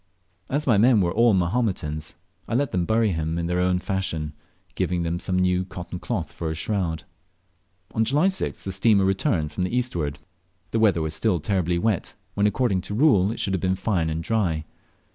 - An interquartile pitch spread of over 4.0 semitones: Yes, average, 4.6 semitones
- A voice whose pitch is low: Yes, very low, 95 Hz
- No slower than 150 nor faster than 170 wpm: No, average, 200 wpm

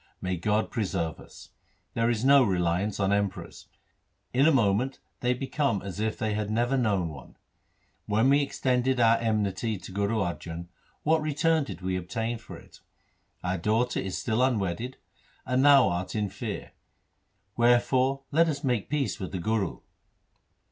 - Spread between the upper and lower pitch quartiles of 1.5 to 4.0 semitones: No, average, 5.0 semitones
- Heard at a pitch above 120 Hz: No, low, 110 Hz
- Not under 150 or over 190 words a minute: Yes, average, 160 wpm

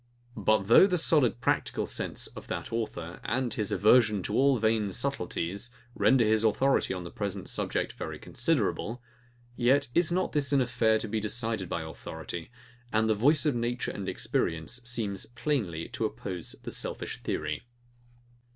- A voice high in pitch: No, low, 110 Hz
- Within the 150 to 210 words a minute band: Yes, average, 165 wpm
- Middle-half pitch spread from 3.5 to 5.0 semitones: Yes, average, 4.2 semitones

